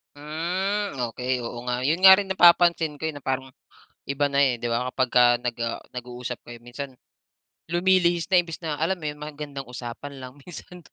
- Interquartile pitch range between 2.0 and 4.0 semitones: No, wide, 5.6 semitones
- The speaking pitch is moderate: Yes, medium, 145 Hz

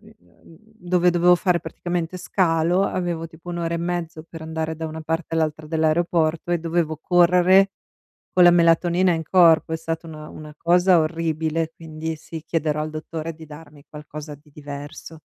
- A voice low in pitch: No, medium, 165 Hz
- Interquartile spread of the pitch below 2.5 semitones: Yes, narrow, 1.8 semitones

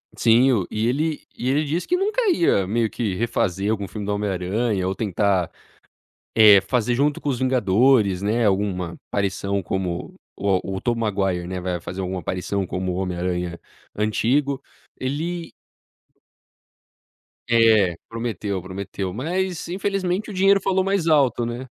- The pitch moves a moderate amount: No, wide, 6.2 semitones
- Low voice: Yes, low, 110 Hz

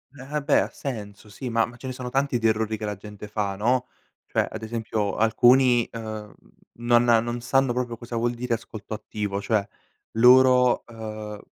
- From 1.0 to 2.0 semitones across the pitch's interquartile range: No, narrow, 2.5 semitones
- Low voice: Yes, low, 115 Hz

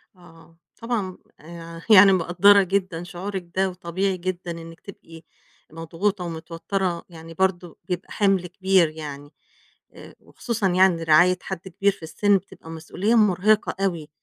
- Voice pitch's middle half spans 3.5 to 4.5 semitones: No, average, 2.7 semitones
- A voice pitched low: No, medium, 180 Hz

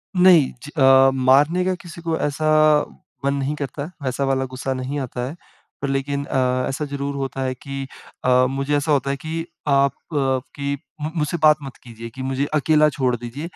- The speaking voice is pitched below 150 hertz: Yes, medium, 140 Hz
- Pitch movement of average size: No, narrow, 2.1 semitones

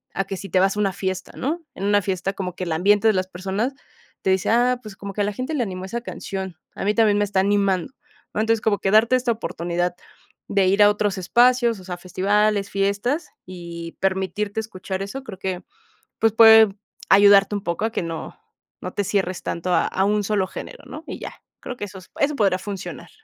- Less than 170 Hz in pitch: No, high, 200 Hz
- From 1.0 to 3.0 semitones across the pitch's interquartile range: Yes, narrow, 2.4 semitones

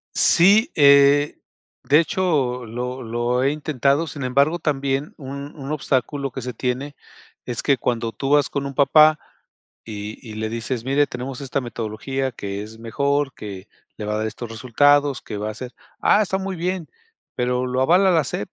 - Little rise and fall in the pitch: No, average, 3.4 semitones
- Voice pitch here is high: No, low, 135 Hz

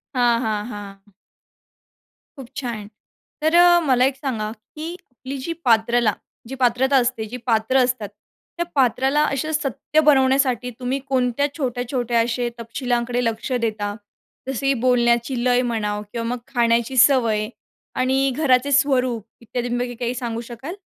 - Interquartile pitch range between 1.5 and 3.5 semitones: Yes, narrow, 2.4 semitones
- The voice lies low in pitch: No, high, 245 Hz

